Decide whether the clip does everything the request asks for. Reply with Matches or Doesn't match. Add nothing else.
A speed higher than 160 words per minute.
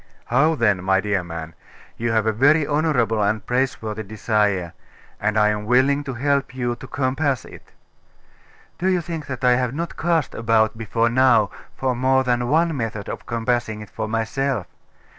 Matches